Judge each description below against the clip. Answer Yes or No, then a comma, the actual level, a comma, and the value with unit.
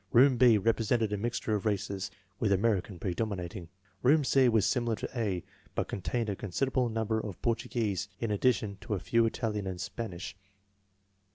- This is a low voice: Yes, low, 110 Hz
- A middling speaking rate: Yes, average, 165 wpm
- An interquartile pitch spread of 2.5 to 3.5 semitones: Yes, average, 3.0 semitones